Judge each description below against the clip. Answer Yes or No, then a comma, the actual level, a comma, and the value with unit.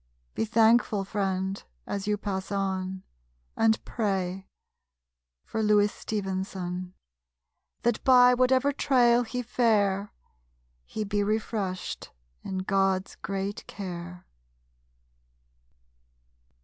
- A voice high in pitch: Yes, high, 200 Hz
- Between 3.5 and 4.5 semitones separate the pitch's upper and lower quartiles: No, average, 2.7 semitones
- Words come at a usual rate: No, slow, 90 wpm